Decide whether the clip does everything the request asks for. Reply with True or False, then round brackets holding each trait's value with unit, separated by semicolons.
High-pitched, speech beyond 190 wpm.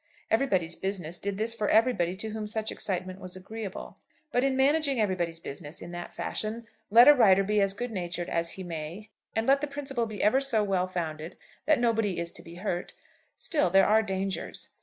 True (200 Hz; 200 wpm)